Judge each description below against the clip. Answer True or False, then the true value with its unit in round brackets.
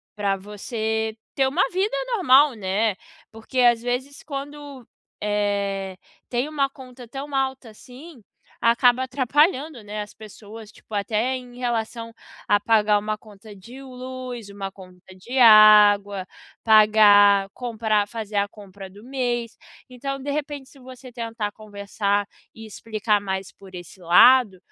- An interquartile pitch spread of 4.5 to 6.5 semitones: False (3.9 semitones)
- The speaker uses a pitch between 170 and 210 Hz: False (225 Hz)